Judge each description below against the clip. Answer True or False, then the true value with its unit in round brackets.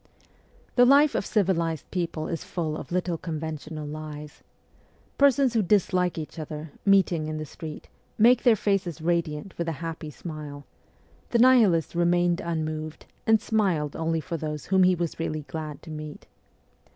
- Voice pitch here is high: False (165 Hz)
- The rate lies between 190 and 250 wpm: False (160 wpm)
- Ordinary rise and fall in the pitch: True (3.4 semitones)